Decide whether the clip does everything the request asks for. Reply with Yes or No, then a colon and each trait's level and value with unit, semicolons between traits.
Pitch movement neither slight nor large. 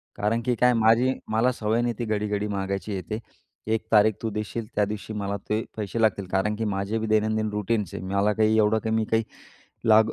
No: narrow, 1.3 semitones